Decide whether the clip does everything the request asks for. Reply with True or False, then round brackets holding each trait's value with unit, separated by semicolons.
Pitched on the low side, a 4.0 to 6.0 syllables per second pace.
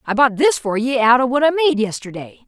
False (245 Hz; 5.7 syllables/s)